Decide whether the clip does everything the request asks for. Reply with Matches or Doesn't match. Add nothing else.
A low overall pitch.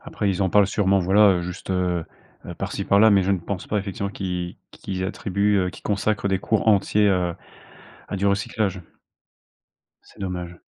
Matches